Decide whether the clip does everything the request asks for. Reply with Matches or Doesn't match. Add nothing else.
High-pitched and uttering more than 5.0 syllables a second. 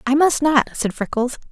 Doesn't match